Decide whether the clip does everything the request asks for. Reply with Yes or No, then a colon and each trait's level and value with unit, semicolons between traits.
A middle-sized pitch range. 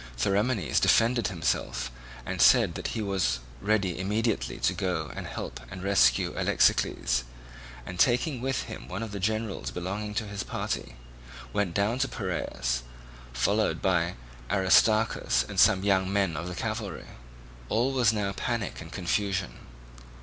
Yes: average, 3.4 semitones